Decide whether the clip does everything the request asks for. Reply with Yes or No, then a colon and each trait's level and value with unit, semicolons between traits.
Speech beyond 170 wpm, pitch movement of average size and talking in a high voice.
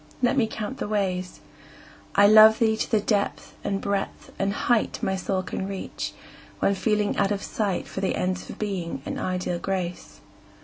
No: average, 180 wpm; narrow, 2.3 semitones; high, 200 Hz